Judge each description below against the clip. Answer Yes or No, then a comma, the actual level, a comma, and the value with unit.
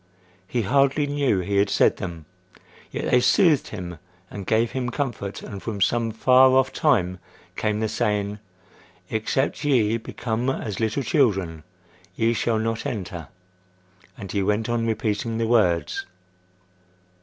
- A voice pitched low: Yes, low, 110 Hz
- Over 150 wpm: No, average, 145 wpm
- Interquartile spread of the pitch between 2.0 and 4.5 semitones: Yes, average, 3.6 semitones